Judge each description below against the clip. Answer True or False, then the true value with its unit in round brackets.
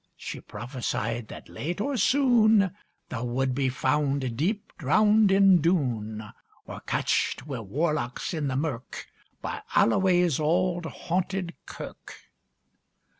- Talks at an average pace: False (120 wpm)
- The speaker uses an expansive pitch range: True (6.7 semitones)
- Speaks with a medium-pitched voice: True (155 Hz)